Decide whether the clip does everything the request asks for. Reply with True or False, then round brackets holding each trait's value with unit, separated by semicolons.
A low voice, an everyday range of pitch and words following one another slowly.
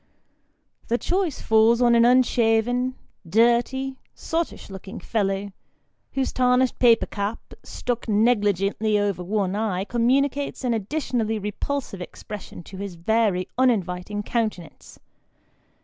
False (225 Hz; 3.6 semitones; 110 wpm)